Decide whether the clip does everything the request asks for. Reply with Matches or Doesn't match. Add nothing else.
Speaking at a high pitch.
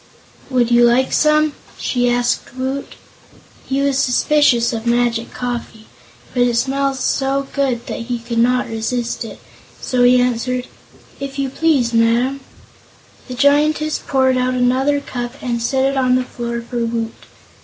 Matches